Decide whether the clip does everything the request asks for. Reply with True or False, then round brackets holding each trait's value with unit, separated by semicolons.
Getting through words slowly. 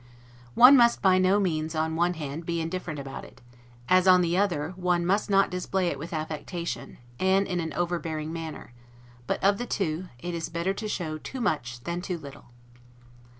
False (190 wpm)